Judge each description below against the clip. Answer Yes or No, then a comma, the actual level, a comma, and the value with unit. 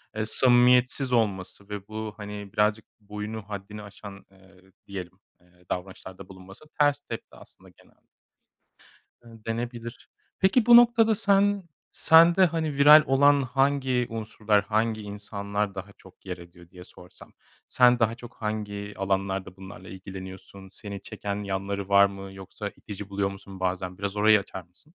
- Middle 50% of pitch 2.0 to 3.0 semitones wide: No, average, 4.0 semitones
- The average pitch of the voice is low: Yes, low, 105 Hz